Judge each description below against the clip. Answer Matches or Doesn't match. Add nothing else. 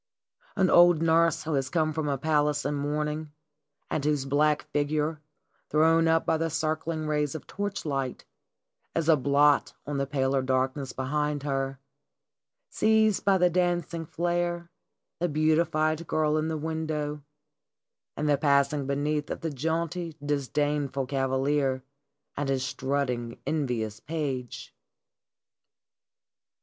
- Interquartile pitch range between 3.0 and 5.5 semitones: Doesn't match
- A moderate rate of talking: Doesn't match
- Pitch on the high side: Doesn't match